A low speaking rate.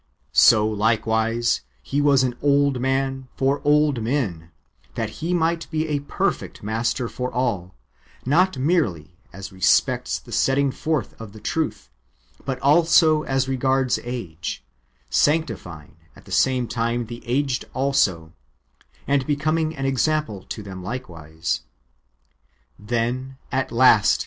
Yes: slow, 130 wpm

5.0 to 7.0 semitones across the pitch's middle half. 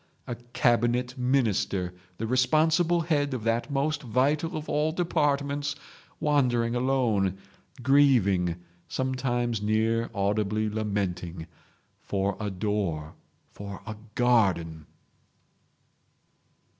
Yes: wide, 5.5 semitones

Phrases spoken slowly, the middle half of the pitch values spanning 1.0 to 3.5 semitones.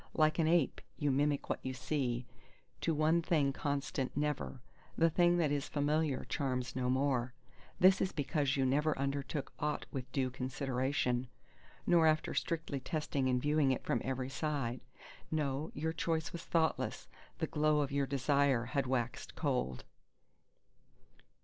No: average, 150 wpm; average, 2.9 semitones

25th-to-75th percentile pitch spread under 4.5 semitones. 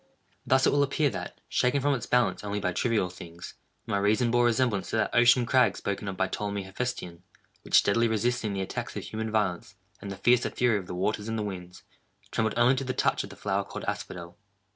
Yes: average, 3.9 semitones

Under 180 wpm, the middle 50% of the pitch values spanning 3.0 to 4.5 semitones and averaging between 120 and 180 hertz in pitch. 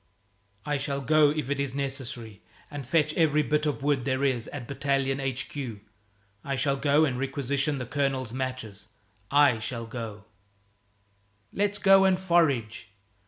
Yes: average, 150 wpm; average, 3.4 semitones; low, 135 Hz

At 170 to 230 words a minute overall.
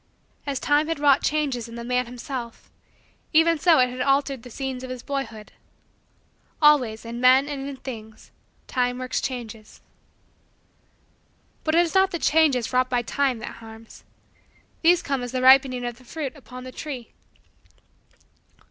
No: average, 160 wpm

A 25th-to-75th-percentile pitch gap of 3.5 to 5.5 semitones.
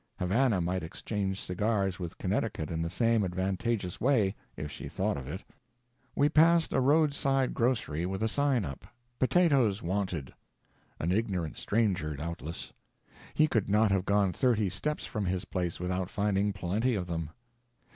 Yes: average, 4.6 semitones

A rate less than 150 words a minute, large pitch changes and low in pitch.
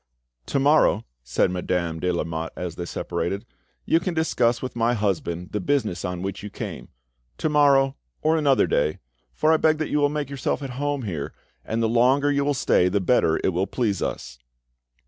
No: average, 195 wpm; wide, 8.0 semitones; low, 115 Hz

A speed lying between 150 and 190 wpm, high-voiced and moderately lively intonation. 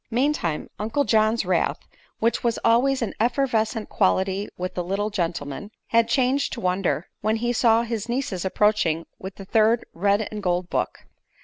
Yes: average, 165 wpm; high, 215 Hz; average, 3.7 semitones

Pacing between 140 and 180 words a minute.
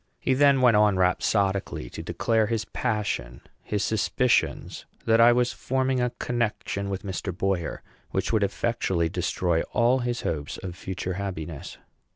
Yes: average, 150 wpm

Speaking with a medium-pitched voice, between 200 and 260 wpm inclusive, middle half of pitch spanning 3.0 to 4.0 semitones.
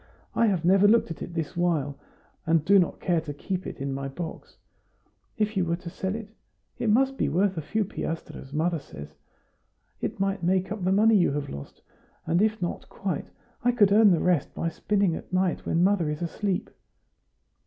Yes: medium, 180 Hz; fast, 205 wpm; average, 3.7 semitones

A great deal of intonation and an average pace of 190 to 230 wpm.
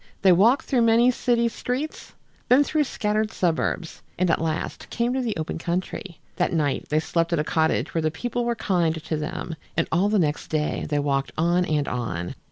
Yes: wide, 6.7 semitones; fast, 205 wpm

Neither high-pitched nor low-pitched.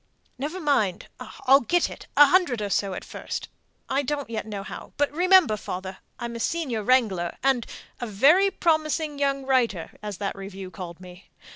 No: high, 245 Hz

